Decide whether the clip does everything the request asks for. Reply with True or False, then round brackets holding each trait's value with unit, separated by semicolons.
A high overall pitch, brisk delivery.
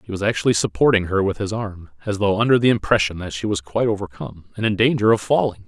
False (105 Hz; 245 wpm)